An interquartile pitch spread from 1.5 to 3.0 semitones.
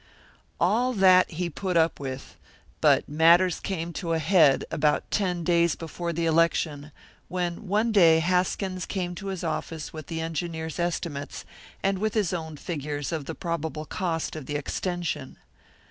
Yes: narrow, 2.4 semitones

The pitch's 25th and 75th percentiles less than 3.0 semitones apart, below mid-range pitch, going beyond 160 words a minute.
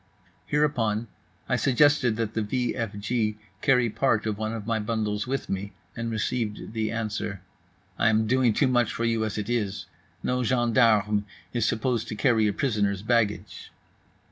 Yes: narrow, 2.4 semitones; low, 115 Hz; average, 170 wpm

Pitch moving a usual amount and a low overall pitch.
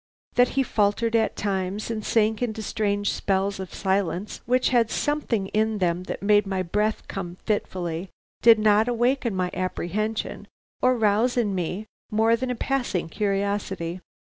No: average, 3.1 semitones; high, 210 Hz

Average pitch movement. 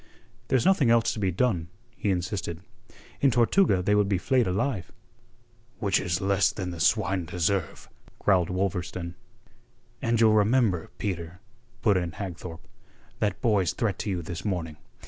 Yes: average, 3.5 semitones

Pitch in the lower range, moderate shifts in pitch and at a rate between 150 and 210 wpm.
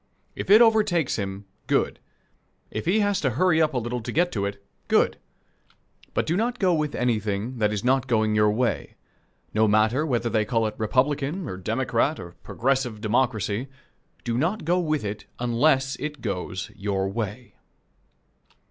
No: low, 125 Hz; wide, 6.2 semitones; average, 165 wpm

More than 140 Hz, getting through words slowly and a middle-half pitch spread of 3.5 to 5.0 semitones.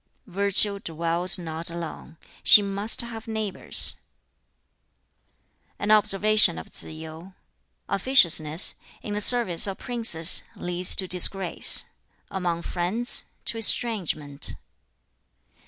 Yes: medium, 185 Hz; slow, 100 wpm; average, 4.2 semitones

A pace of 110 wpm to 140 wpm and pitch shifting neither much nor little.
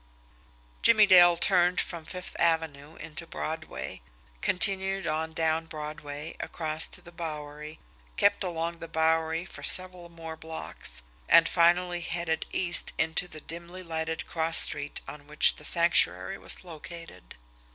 No: slow, 135 wpm; narrow, 1.8 semitones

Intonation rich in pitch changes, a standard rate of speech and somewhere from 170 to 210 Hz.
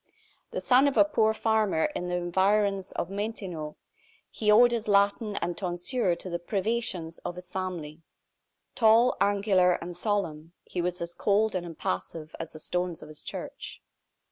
No: average, 3.7 semitones; average, 165 wpm; medium, 185 Hz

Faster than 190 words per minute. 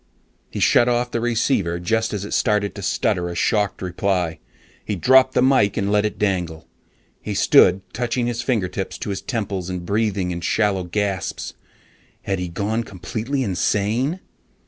No: average, 165 wpm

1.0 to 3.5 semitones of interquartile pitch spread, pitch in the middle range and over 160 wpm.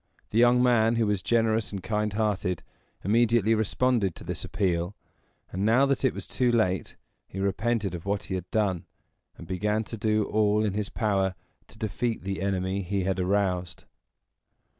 No: average, 2.9 semitones; low, 105 Hz; average, 175 wpm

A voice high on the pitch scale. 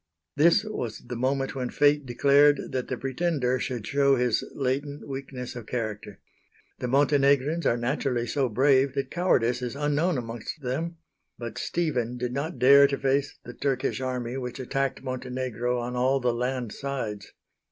No: low, 130 Hz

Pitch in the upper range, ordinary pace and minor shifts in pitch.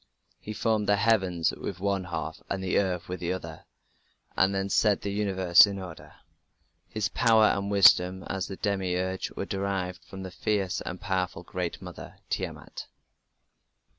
No: very low, 95 Hz; average, 160 wpm; narrow, 1.8 semitones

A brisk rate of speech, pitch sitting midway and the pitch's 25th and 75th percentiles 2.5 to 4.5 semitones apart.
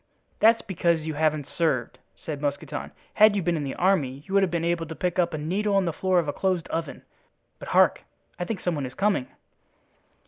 Yes: fast, 220 wpm; medium, 170 Hz; average, 3.7 semitones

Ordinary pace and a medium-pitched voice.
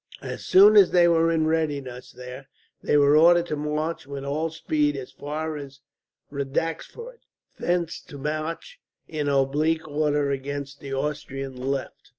Yes: average, 150 wpm; medium, 150 Hz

